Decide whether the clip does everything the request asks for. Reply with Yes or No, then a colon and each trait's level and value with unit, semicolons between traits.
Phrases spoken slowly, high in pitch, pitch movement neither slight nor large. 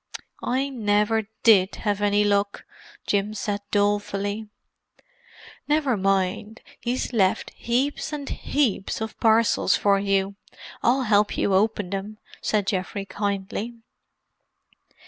No: slow, 105 wpm; high, 205 Hz; narrow, 2.1 semitones